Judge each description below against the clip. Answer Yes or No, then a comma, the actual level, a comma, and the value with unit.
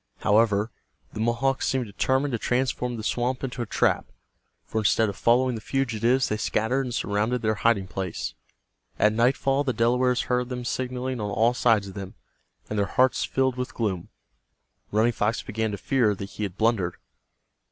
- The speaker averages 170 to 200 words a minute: Yes, average, 175 wpm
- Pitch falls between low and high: No, low, 115 Hz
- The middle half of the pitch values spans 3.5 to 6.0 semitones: No, average, 3.0 semitones